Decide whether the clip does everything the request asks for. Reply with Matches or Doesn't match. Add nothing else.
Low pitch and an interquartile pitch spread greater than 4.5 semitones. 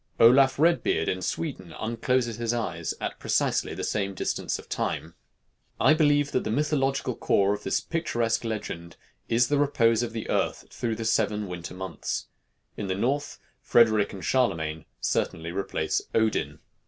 Matches